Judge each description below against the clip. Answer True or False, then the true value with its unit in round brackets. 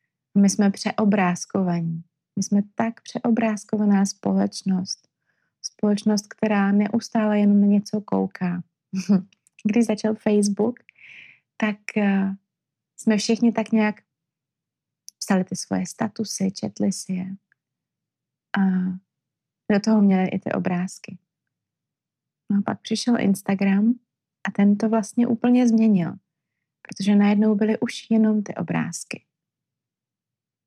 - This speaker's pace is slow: True (110 wpm)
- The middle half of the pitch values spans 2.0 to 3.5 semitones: True (3.2 semitones)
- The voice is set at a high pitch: True (200 Hz)